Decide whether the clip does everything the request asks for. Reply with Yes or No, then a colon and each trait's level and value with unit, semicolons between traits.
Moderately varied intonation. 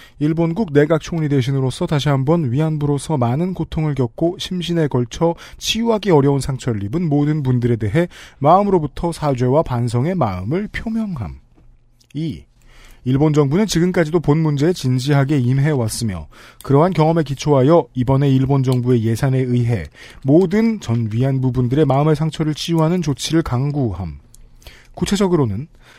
Yes: average, 4.7 semitones